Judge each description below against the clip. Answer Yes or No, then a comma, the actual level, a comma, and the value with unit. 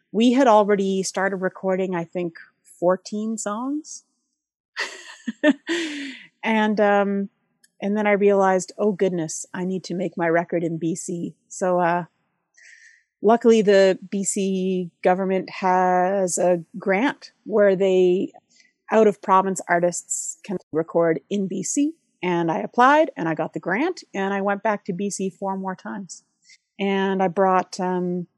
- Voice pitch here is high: Yes, high, 195 Hz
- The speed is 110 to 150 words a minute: Yes, slow, 135 wpm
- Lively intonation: No, average, 2.9 semitones